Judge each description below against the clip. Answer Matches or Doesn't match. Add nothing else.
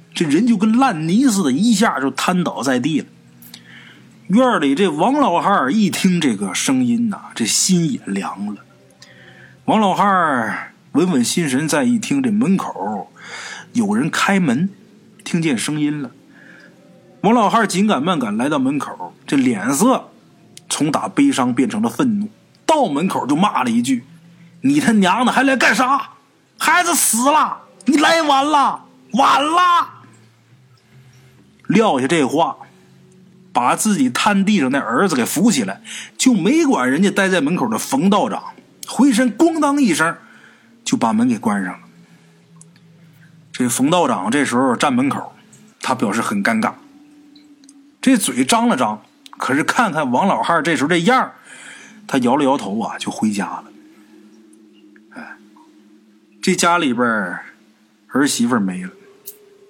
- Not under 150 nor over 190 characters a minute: Doesn't match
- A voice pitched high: Matches